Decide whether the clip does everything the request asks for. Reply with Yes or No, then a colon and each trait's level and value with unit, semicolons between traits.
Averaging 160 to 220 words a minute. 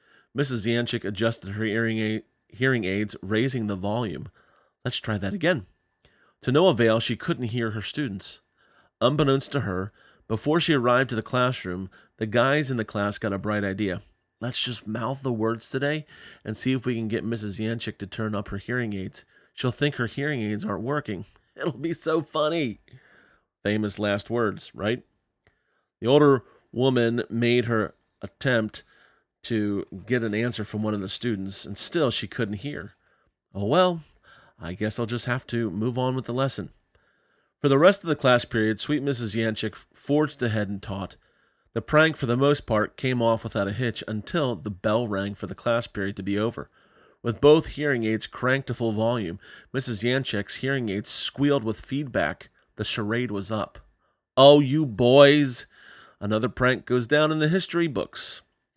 Yes: average, 175 wpm